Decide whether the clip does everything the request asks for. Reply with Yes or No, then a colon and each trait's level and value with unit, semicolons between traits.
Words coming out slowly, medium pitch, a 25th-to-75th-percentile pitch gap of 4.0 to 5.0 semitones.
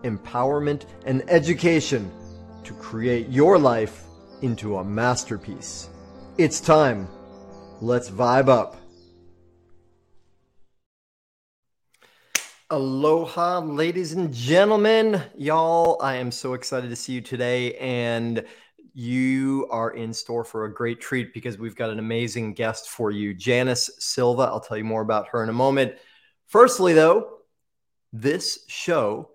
No: slow, 125 wpm; low, 120 Hz; average, 4.7 semitones